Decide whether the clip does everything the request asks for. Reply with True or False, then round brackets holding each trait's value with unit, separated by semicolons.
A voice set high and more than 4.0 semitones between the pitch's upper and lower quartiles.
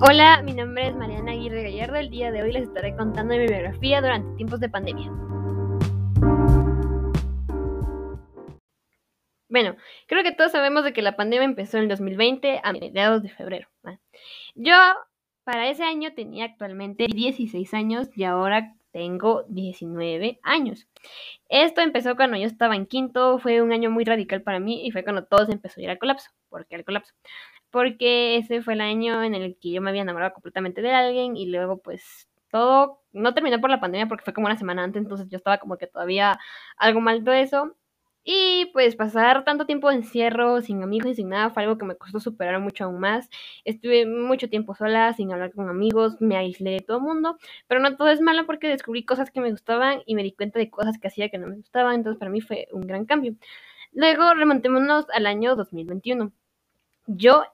True (225 Hz; 4.7 semitones)